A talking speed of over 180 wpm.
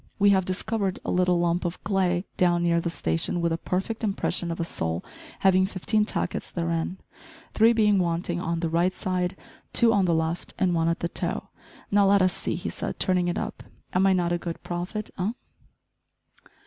Yes: average, 200 wpm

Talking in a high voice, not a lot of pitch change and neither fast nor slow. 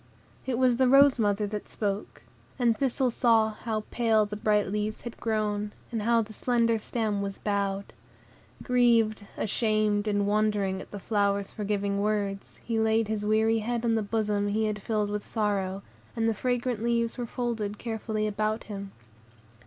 Yes: high, 215 Hz; narrow, 1.9 semitones; average, 170 wpm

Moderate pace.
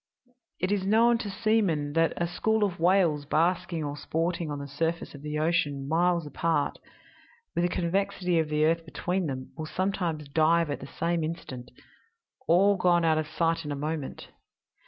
Yes: average, 175 wpm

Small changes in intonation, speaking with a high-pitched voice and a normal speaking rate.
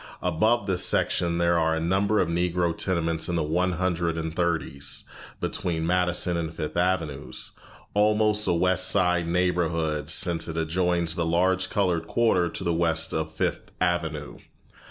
No: narrow, 1.9 semitones; very low, 85 Hz; average, 155 wpm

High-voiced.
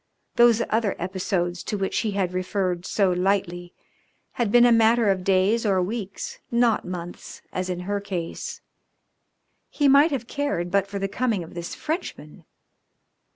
Yes: high, 195 Hz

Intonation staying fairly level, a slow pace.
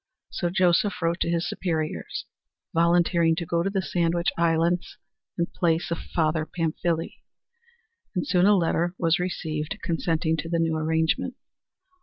No: narrow, 1.3 semitones; average, 145 wpm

